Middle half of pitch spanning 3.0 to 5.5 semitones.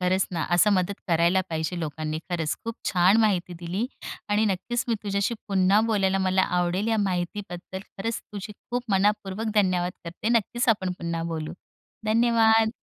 Yes: average, 3.5 semitones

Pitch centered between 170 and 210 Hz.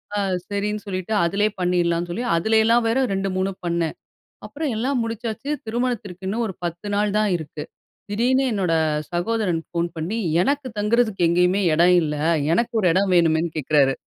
Yes: high, 195 Hz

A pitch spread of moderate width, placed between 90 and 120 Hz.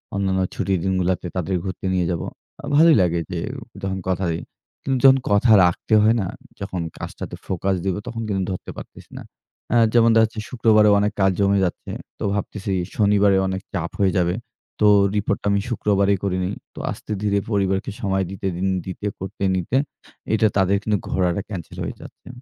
No: narrow, 1.9 semitones; low, 100 Hz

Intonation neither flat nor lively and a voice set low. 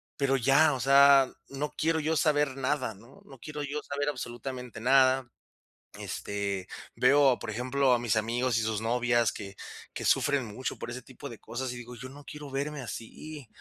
Yes: average, 3.1 semitones; low, 130 Hz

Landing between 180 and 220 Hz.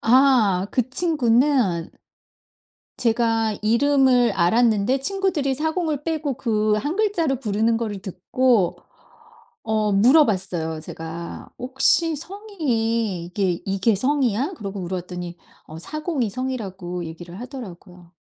No: high, 230 Hz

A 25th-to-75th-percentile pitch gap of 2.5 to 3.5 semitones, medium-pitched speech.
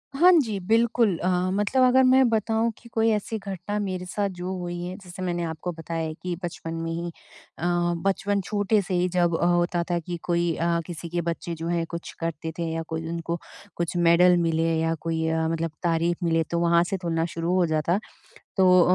Yes: average, 2.8 semitones; medium, 175 Hz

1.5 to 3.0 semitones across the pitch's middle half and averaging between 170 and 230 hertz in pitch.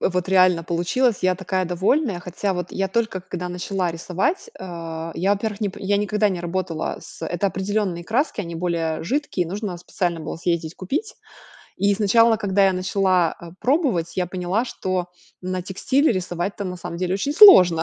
Yes: average, 2.7 semitones; medium, 185 Hz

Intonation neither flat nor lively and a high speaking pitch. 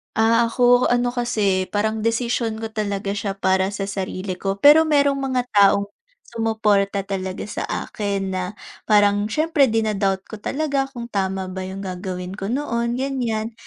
Yes: average, 3.6 semitones; high, 215 Hz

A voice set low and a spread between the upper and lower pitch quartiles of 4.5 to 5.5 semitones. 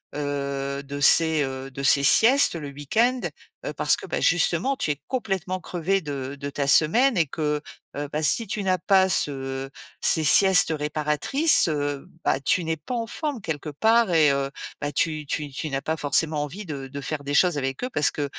No: medium, 150 Hz; average, 4.8 semitones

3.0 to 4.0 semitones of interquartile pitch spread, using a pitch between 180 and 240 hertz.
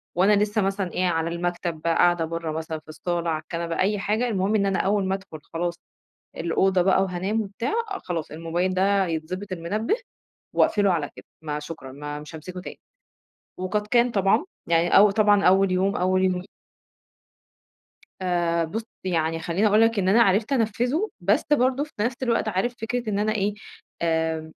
Yes: average, 3.7 semitones; medium, 185 Hz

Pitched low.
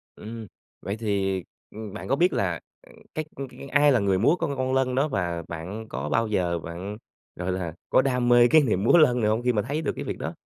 Yes: low, 110 Hz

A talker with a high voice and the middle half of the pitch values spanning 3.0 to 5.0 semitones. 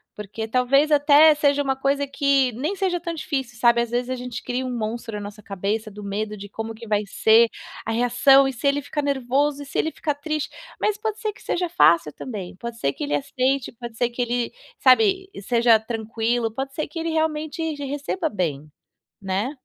Yes: very high, 250 Hz; average, 4.5 semitones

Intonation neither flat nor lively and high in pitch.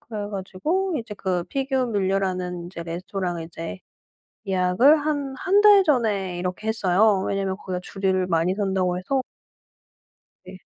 Yes: average, 4.3 semitones; high, 195 Hz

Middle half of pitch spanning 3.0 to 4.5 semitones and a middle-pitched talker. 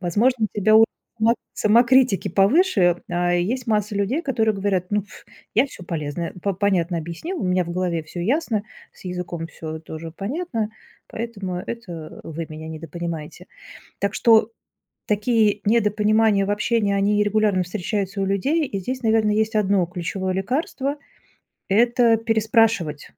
No: average, 4.1 semitones; high, 205 Hz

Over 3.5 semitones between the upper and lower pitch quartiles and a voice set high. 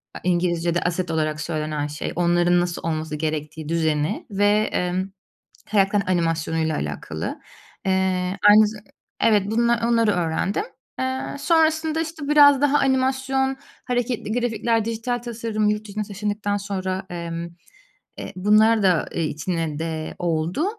Yes: wide, 5.5 semitones; high, 195 Hz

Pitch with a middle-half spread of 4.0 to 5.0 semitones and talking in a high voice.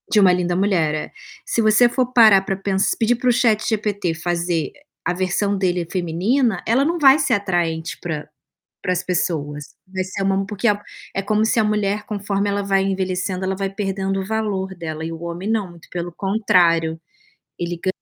No: average, 3.2 semitones; high, 195 Hz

